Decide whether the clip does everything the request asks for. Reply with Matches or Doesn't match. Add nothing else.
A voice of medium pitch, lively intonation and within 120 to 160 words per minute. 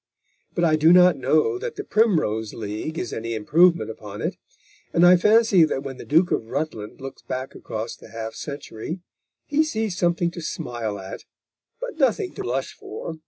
Doesn't match